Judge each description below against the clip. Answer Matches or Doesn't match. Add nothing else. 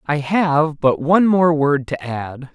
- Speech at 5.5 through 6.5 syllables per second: Doesn't match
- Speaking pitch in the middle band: Matches